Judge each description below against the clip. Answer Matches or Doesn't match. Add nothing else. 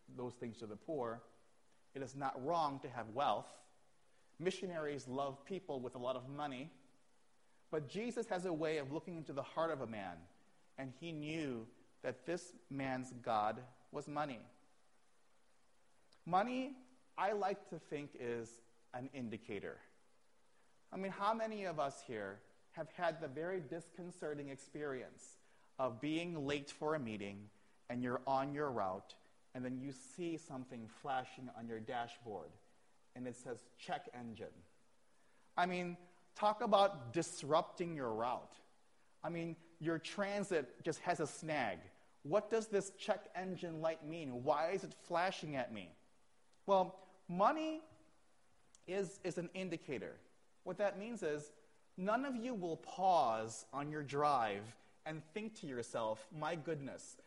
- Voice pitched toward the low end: Doesn't match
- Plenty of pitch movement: Matches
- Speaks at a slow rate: Doesn't match